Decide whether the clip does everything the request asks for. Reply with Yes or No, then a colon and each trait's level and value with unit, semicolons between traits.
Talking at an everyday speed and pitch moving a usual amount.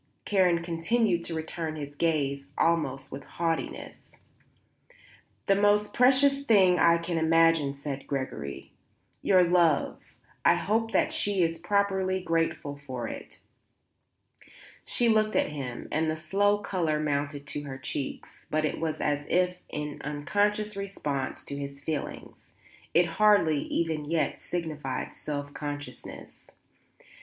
No: slow, 130 wpm; average, 4.6 semitones